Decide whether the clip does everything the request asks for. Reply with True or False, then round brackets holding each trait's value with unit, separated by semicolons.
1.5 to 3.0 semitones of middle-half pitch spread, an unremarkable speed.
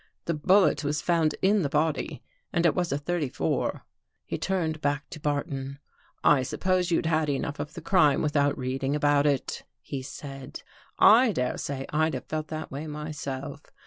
True (2.5 semitones; 190 wpm)